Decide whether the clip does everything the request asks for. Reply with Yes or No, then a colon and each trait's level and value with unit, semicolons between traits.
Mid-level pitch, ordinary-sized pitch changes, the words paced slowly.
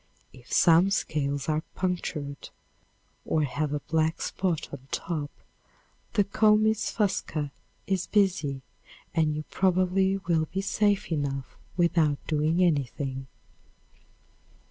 Yes: medium, 160 Hz; average, 4.7 semitones; slow, 110 wpm